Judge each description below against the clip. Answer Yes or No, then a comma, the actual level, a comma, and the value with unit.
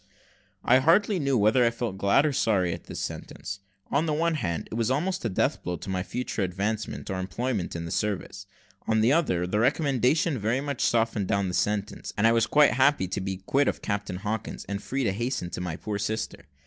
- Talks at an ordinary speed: No, fast, 220 wpm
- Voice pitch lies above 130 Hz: No, low, 110 Hz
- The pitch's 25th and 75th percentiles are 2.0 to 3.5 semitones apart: No, wide, 5.4 semitones